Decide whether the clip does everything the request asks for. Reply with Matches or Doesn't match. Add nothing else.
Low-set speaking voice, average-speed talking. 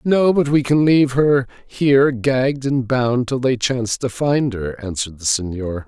Matches